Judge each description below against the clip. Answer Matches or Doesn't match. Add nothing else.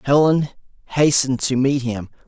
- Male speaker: Matches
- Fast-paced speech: Doesn't match